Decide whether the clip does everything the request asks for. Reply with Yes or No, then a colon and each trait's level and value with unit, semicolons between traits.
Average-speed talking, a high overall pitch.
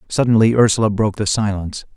No: average, 155 wpm; low, 105 Hz